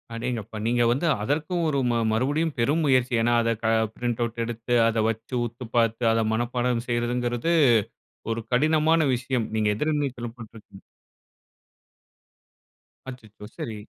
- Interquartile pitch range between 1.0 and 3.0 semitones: Yes, narrow, 2.6 semitones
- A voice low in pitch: Yes, low, 120 Hz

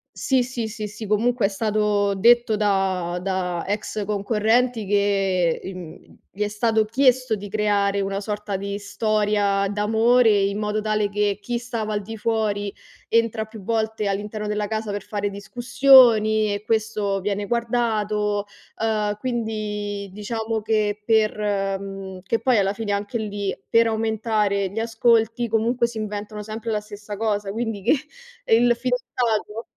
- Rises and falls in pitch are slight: Yes, narrow, 1.8 semitones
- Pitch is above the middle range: Yes, high, 210 Hz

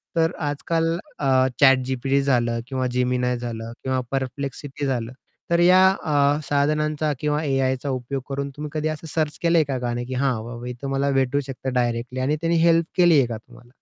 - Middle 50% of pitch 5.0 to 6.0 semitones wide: No, average, 3.2 semitones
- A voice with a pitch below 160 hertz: Yes, low, 135 Hz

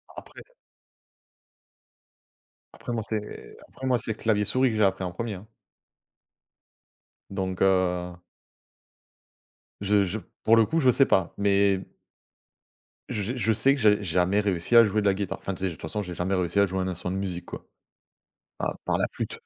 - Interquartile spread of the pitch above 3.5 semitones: No, average, 3.0 semitones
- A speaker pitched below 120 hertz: Yes, low, 100 Hz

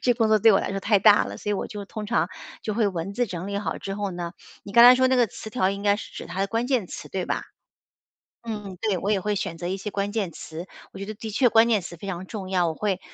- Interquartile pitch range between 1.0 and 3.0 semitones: Yes, narrow, 2.6 semitones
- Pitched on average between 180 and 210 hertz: Yes, high, 200 Hz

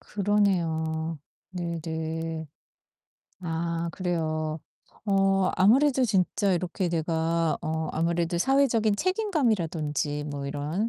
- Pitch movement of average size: Yes, average, 3.7 semitones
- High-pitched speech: No, medium, 170 Hz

